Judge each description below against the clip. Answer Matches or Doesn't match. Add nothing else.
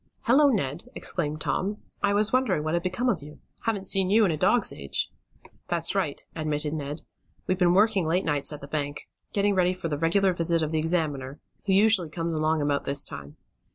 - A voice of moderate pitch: Matches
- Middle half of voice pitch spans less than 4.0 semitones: Doesn't match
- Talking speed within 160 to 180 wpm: Doesn't match